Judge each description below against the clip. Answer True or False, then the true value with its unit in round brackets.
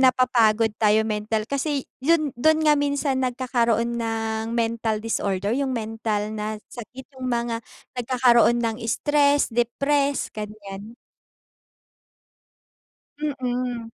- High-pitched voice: True (235 Hz)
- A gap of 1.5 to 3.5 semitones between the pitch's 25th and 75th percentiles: True (3.1 semitones)